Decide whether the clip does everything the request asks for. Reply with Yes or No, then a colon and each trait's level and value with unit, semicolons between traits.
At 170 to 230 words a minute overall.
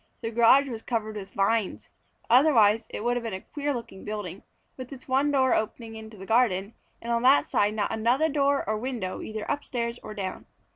Yes: average, 200 wpm